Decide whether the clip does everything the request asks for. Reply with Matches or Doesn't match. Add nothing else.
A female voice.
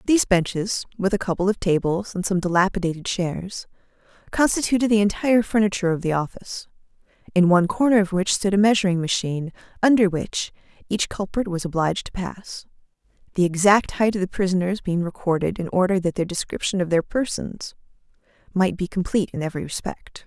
Matches